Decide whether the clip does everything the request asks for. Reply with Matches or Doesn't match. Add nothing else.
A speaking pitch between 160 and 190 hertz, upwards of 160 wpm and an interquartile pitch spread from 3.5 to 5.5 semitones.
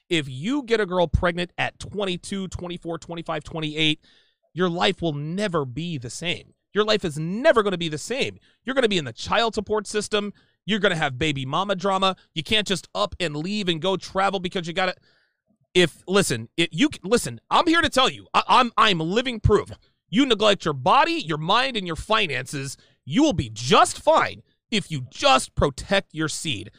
Matches